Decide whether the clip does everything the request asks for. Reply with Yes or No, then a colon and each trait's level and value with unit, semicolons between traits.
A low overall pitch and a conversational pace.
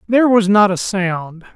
No: high, 200 Hz; average, 195 wpm